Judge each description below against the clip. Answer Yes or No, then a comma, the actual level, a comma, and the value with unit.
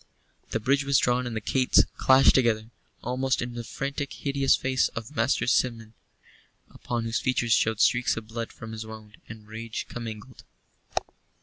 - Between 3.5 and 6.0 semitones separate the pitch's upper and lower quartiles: No, average, 2.7 semitones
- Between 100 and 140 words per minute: No, average, 165 wpm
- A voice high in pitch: No, low, 120 Hz